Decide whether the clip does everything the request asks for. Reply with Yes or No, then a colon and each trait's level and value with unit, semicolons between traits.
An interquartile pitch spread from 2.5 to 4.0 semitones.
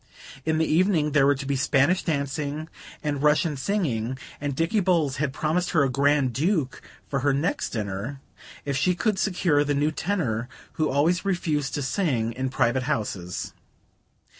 Yes: average, 3.6 semitones